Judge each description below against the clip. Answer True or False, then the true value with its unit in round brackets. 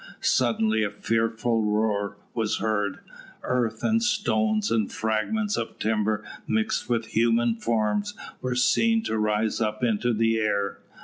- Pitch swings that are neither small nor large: False (1.7 semitones)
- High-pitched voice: False (110 Hz)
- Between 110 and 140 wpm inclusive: True (135 wpm)